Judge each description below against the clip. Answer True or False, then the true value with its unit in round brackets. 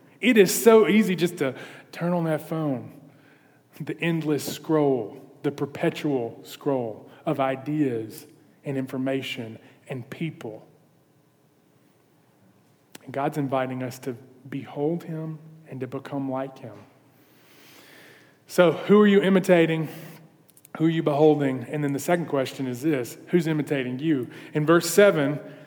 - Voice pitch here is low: False (145 Hz)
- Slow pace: True (130 wpm)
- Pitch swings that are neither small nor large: True (3.2 semitones)